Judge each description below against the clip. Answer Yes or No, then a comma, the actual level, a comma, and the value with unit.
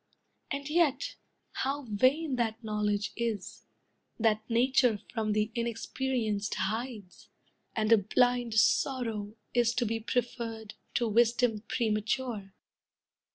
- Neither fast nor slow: No, slow, 110 wpm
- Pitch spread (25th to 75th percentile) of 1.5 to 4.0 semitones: Yes, average, 2.7 semitones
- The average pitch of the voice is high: Yes, high, 230 Hz